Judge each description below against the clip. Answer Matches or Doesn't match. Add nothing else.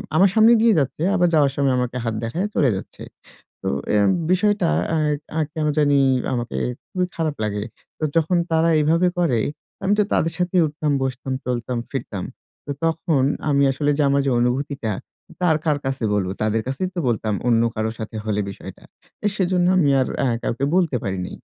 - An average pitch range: Doesn't match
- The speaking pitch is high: Doesn't match